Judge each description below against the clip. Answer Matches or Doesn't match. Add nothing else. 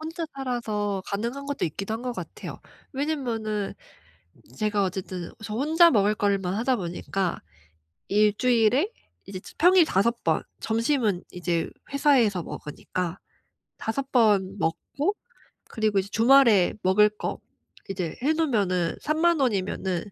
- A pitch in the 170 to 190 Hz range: Doesn't match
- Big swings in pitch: Matches